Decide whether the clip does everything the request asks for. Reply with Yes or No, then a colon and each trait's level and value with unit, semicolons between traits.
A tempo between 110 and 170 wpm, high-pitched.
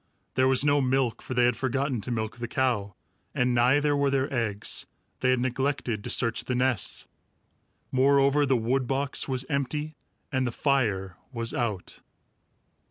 No: average, 165 wpm; low, 130 Hz